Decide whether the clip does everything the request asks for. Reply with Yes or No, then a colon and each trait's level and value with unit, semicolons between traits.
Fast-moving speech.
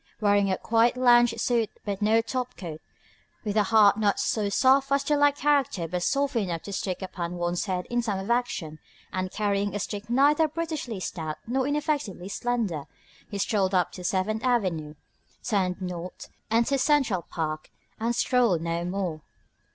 No: average, 170 wpm